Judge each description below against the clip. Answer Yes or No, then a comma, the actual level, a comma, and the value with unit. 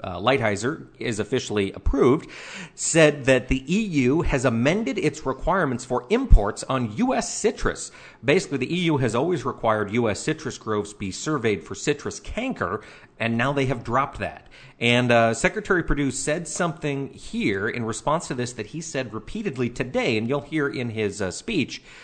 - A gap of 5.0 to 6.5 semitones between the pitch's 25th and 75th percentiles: Yes, wide, 5.4 semitones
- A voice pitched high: No, low, 130 Hz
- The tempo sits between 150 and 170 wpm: Yes, average, 165 wpm